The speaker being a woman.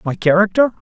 No: male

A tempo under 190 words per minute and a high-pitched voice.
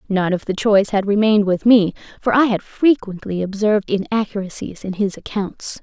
Yes: average, 175 wpm; high, 205 Hz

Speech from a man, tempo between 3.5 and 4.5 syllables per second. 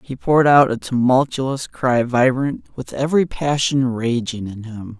Yes: male; 4.3 syllables/s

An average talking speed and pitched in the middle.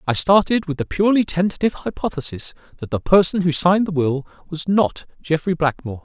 Yes: average, 180 wpm; medium, 170 Hz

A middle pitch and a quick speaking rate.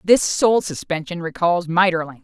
No: medium, 175 Hz; slow, 135 wpm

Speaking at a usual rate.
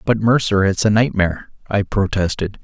Yes: average, 160 wpm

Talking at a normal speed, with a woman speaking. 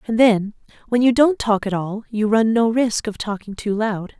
No: fast, 230 wpm; female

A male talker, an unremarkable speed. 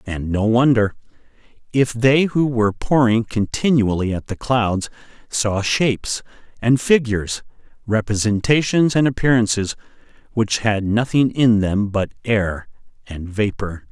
No: male; slow, 120 wpm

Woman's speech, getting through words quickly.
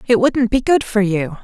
Yes: female; fast, 250 wpm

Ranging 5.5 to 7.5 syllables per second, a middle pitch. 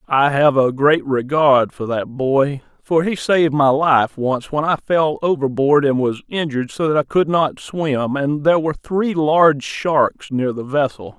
No: 4.3 syllables/s; medium, 145 Hz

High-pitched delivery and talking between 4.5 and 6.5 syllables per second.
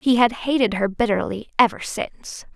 Yes: high, 230 Hz; 5.1 syllables/s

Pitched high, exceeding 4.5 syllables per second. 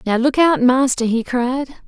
No: very high, 255 Hz; 4.3 syllables/s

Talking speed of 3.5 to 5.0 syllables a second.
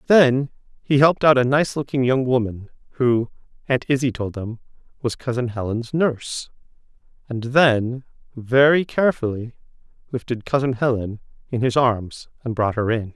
Yes: 4.8 syllables/s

